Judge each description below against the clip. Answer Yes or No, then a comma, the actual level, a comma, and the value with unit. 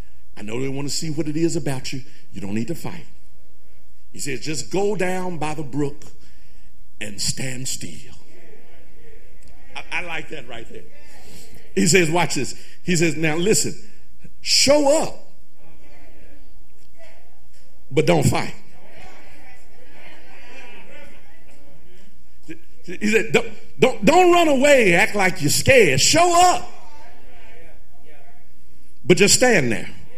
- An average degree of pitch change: No, wide, 7.0 semitones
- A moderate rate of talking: No, slow, 125 wpm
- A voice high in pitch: No, medium, 155 Hz